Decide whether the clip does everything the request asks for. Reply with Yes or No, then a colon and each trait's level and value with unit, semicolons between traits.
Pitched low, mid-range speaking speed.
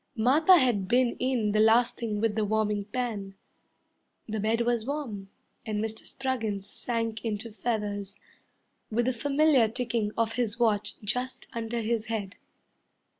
No: high, 225 Hz; average, 145 wpm